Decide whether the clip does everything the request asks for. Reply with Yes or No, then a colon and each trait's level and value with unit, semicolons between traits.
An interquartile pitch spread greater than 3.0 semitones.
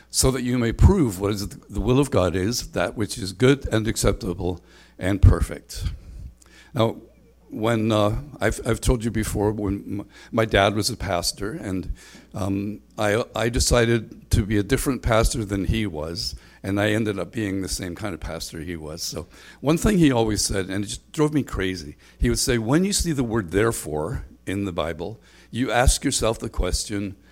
Yes: average, 3.9 semitones